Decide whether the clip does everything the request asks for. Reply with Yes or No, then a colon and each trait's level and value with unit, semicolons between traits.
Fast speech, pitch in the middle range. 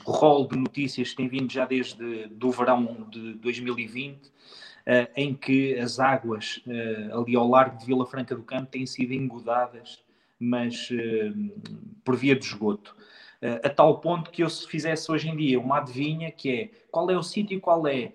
No: fast, 190 wpm; low, 130 Hz